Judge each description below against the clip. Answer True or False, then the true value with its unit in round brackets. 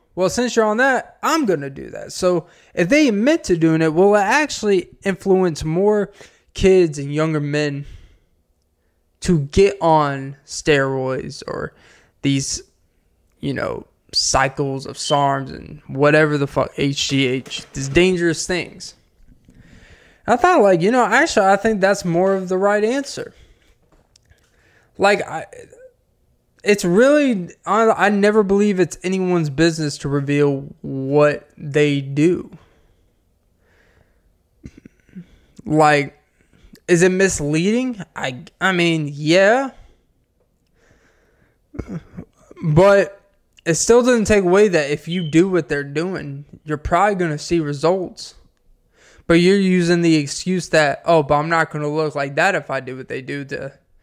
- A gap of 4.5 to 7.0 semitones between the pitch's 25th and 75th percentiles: True (5.2 semitones)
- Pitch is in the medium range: True (165 Hz)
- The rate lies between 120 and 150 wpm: True (135 wpm)